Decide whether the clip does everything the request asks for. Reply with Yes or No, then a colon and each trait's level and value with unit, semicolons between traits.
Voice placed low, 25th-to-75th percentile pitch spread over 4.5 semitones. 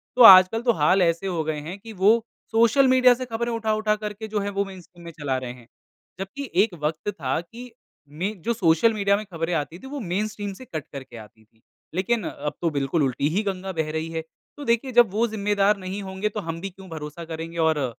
No: high, 190 Hz; average, 5.2 semitones